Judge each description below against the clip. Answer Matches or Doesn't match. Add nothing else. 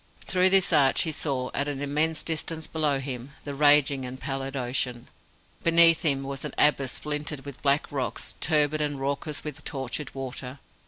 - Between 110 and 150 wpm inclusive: Doesn't match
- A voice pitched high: Doesn't match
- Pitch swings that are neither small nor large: Doesn't match